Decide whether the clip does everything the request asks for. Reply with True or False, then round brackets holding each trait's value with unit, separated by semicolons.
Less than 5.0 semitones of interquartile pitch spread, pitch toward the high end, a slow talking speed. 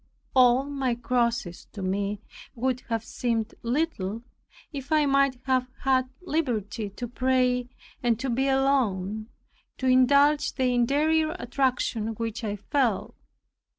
True (3.2 semitones; 250 Hz; 125 wpm)